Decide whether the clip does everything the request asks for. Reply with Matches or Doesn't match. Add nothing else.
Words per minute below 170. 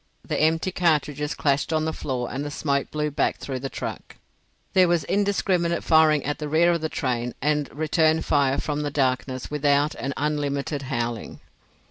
Doesn't match